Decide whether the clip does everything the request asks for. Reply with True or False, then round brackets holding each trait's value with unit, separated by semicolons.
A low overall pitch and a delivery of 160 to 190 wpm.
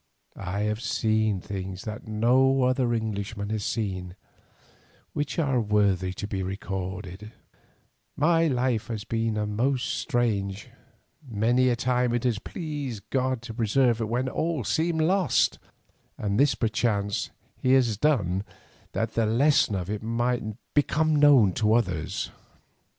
False (115 Hz; 135 wpm)